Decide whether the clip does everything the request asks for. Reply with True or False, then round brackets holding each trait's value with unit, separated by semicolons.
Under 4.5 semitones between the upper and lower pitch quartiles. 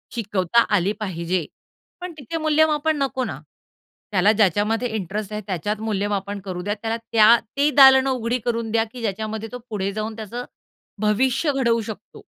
True (3.4 semitones)